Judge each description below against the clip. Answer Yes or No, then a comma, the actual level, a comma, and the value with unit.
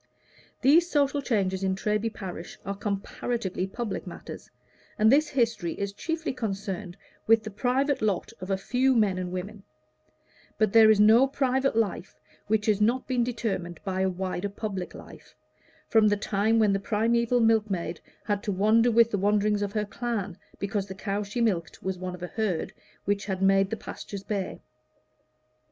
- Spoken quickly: No, average, 175 wpm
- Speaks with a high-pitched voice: Yes, high, 210 Hz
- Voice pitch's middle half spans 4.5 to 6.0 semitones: No, average, 3.1 semitones